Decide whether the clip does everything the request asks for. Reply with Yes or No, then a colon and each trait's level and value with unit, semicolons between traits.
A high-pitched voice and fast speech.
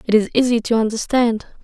No: high, 230 Hz; average, 185 wpm